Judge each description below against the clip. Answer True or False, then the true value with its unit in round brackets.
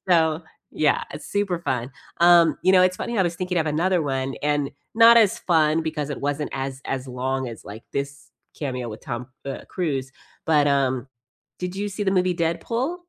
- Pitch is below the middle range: False (155 Hz)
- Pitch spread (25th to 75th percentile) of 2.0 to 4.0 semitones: False (5.1 semitones)